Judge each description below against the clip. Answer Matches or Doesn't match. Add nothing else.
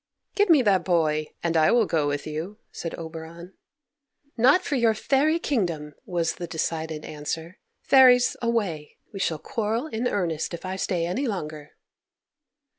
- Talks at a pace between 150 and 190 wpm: Matches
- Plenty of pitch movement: Matches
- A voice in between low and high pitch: Matches